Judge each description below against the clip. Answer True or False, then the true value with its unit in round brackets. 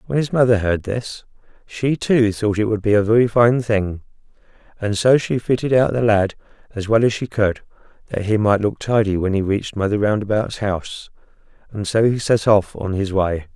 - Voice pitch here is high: False (110 Hz)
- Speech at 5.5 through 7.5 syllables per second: False (5.1 syllables/s)